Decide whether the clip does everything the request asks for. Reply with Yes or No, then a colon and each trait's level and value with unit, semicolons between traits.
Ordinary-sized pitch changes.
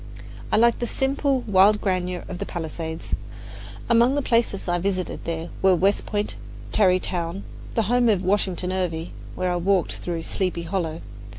Yes: average, 3.4 semitones